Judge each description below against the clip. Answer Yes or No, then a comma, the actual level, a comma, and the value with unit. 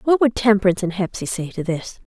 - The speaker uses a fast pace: Yes, fast, 230 wpm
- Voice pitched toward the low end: No, high, 195 Hz